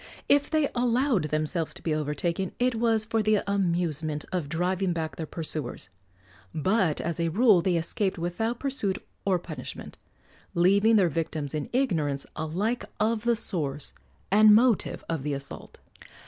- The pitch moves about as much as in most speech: No, wide, 5.7 semitones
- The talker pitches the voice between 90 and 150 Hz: No, medium, 180 Hz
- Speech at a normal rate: Yes, average, 150 wpm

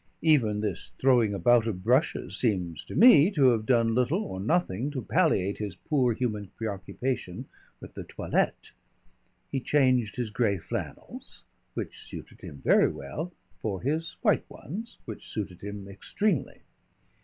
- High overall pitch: No, low, 115 Hz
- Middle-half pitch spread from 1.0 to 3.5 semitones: No, wide, 5.6 semitones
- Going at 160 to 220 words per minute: No, average, 145 wpm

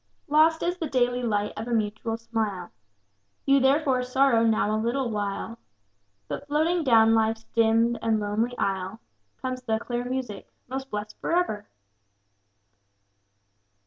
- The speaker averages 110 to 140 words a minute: Yes, slow, 135 wpm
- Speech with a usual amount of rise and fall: Yes, average, 3.4 semitones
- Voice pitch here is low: No, high, 230 Hz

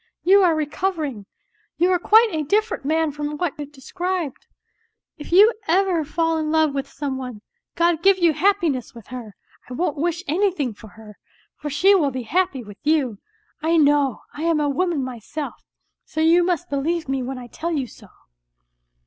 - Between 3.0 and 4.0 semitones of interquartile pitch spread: No, average, 4.4 semitones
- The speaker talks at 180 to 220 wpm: Yes, average, 185 wpm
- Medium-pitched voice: No, very high, 310 Hz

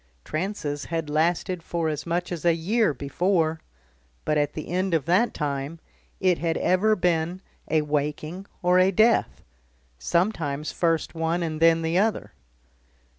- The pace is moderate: Yes, average, 150 wpm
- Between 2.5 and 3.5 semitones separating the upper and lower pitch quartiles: Yes, average, 2.8 semitones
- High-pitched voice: No, medium, 165 Hz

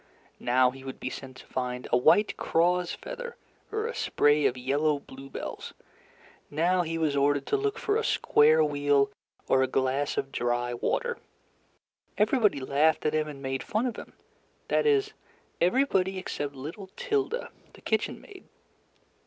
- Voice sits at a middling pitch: Yes, medium, 150 Hz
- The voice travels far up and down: Yes, wide, 7.8 semitones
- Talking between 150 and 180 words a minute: Yes, average, 160 wpm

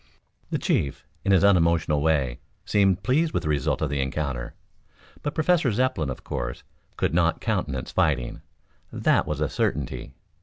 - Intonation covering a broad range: Yes, wide, 6.5 semitones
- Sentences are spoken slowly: No, average, 155 wpm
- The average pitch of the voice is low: Yes, very low, 80 Hz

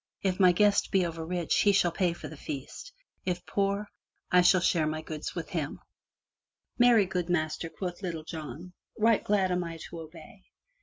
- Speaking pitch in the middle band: Yes, medium, 175 Hz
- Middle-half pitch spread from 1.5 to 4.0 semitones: Yes, average, 2.8 semitones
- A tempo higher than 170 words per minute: Yes, average, 185 wpm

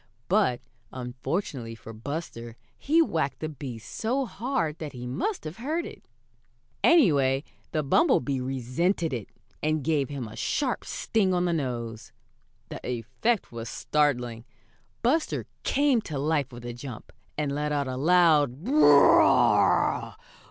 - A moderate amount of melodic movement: No, wide, 6.4 semitones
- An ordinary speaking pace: Yes, average, 145 wpm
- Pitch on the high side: No, medium, 145 Hz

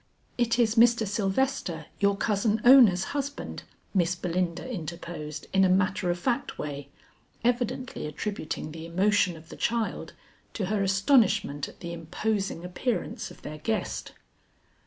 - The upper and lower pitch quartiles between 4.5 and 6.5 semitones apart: Yes, average, 4.9 semitones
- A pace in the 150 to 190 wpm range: No, slow, 135 wpm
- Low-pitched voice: No, high, 195 Hz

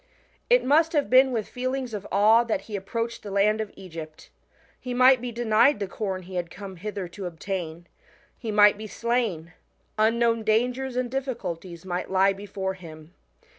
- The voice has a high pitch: Yes, high, 210 Hz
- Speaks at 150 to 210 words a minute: Yes, average, 170 wpm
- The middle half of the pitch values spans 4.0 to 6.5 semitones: Yes, average, 4.4 semitones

